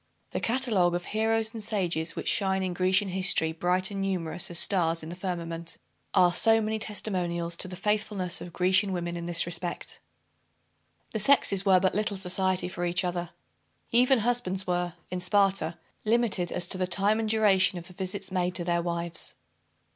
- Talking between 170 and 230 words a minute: Yes, average, 180 wpm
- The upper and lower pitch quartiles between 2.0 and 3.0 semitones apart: Yes, average, 2.7 semitones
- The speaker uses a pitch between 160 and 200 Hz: Yes, medium, 185 Hz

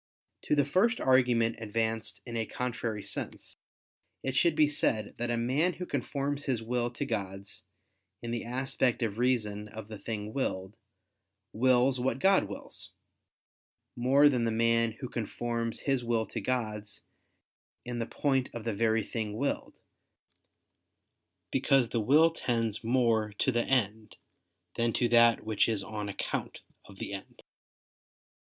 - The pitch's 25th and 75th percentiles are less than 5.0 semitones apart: Yes, average, 2.8 semitones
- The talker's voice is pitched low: Yes, low, 115 Hz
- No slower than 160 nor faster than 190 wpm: No, average, 150 wpm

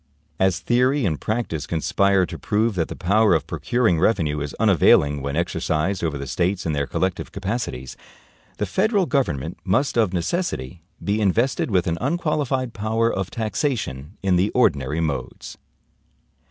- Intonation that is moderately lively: No, wide, 6.4 semitones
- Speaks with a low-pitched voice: Yes, very low, 95 Hz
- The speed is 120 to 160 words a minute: Yes, average, 155 wpm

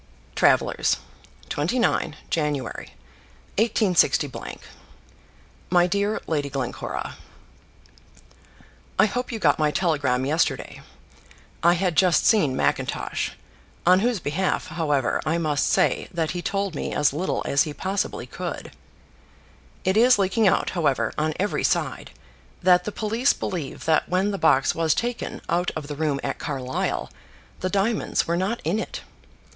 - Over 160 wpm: No, slow, 135 wpm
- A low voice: No, medium, 170 Hz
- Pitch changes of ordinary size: Yes, average, 4.9 semitones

